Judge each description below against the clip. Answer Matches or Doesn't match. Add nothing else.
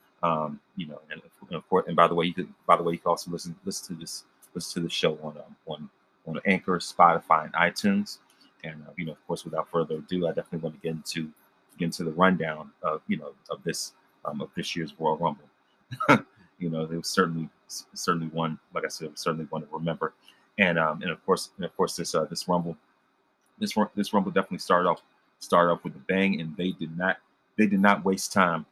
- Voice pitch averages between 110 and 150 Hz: Doesn't match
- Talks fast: Matches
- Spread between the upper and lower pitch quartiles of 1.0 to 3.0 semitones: Matches